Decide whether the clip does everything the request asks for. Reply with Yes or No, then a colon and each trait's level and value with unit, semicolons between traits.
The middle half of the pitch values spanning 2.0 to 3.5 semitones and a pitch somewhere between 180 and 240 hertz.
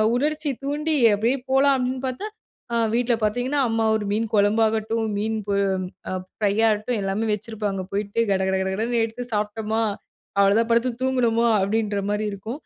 Yes: average, 2.9 semitones; high, 225 Hz